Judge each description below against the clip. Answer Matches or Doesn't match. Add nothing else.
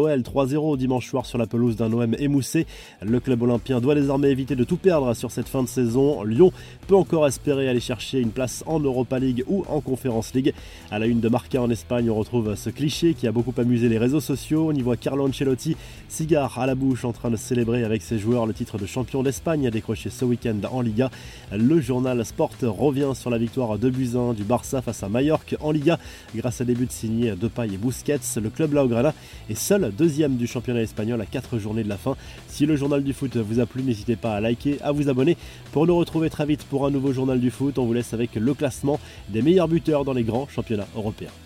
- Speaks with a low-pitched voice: Matches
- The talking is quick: Matches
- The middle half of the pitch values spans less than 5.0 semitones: Matches